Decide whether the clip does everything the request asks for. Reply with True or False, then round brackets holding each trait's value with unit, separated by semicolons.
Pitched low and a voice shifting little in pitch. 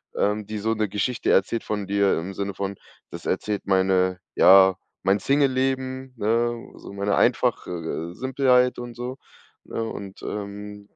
False (105 Hz; 3.9 semitones)